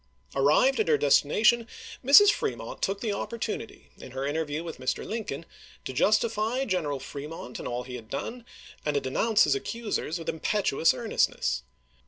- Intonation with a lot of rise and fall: Yes, wide, 8.7 semitones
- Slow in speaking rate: No, average, 160 wpm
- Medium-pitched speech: Yes, medium, 170 Hz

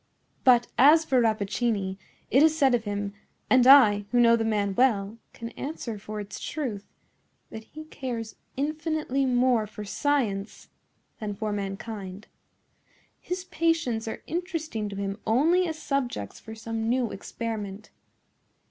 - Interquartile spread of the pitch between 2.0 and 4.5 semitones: No, average, 4.9 semitones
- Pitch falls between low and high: No, high, 230 Hz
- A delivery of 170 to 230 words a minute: No, slow, 135 wpm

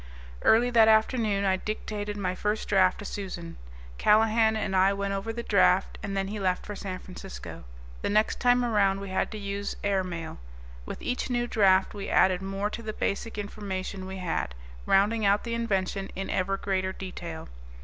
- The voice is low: No, high, 200 Hz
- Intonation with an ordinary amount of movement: No, narrow, 2.3 semitones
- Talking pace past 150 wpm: Yes, average, 185 wpm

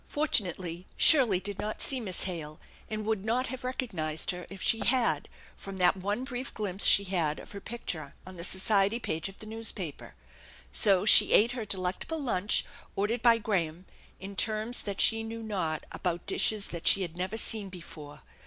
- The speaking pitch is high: Yes, high, 200 Hz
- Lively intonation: No, average, 3.8 semitones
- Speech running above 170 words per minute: Yes, average, 180 wpm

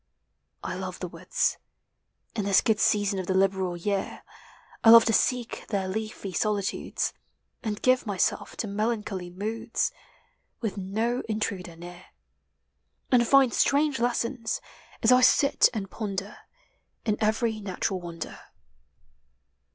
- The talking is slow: Yes, slow, 130 wpm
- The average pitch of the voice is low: No, high, 215 Hz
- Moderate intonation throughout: Yes, average, 3.2 semitones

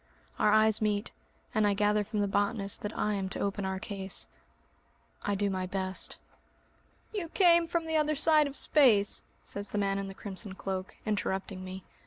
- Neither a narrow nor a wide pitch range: No, narrow, 2.1 semitones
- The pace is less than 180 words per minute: No, average, 185 wpm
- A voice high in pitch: Yes, high, 205 Hz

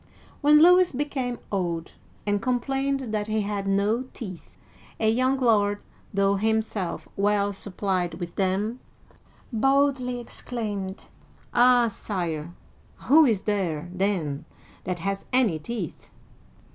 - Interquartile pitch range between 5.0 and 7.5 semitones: No, average, 4.4 semitones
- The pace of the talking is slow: Yes, slow, 120 wpm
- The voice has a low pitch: No, high, 210 Hz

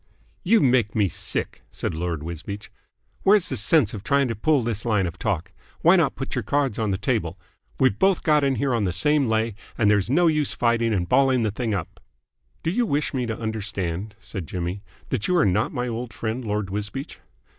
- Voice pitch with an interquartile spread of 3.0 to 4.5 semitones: No, average, 5.1 semitones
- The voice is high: No, low, 110 Hz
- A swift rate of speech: Yes, fast, 210 wpm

